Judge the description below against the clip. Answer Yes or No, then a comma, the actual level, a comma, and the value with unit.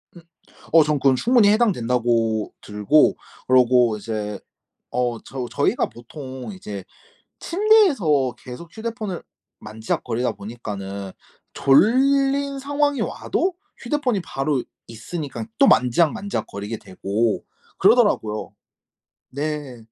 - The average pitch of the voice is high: No, low, 135 Hz